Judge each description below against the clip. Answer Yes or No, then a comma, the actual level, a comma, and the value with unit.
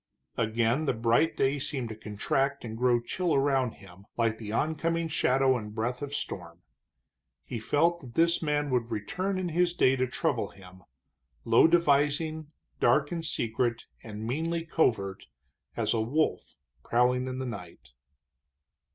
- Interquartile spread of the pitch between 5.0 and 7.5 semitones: Yes, wide, 5.6 semitones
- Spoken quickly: No, average, 150 wpm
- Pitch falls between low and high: No, low, 130 Hz